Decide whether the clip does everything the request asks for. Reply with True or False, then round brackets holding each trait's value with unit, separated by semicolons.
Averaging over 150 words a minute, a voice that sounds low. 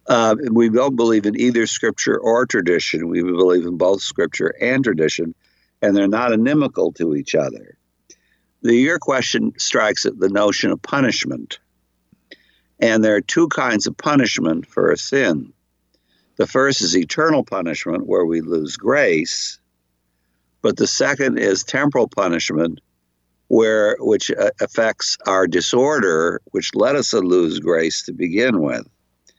False (145 wpm; 85 Hz)